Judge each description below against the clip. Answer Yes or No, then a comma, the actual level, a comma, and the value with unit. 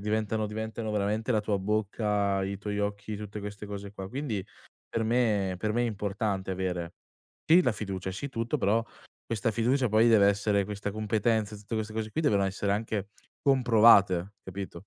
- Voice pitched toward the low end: Yes, low, 105 Hz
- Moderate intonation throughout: No, narrow, 1.9 semitones